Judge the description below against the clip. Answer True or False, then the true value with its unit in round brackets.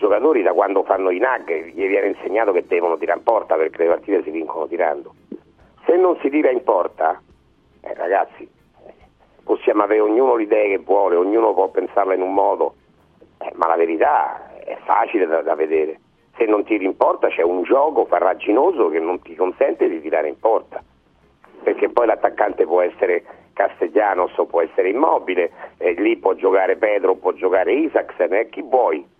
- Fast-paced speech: True (180 wpm)